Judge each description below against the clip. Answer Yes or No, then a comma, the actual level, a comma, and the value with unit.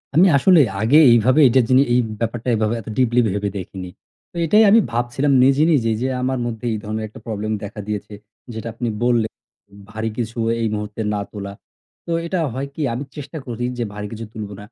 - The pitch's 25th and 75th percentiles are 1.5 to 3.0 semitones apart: No, average, 3.4 semitones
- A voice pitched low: Yes, low, 115 Hz